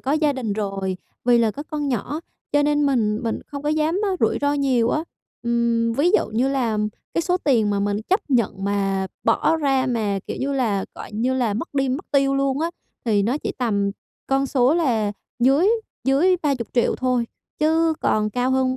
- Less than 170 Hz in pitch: No, very high, 255 Hz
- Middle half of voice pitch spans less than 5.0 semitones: Yes, average, 4.5 semitones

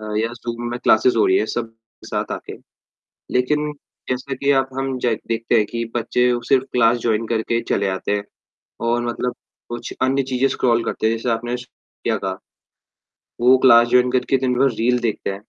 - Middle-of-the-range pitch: No, low, 120 Hz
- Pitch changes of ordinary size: No, narrow, 1.9 semitones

